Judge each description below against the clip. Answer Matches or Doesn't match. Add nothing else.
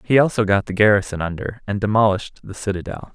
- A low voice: Matches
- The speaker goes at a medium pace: Matches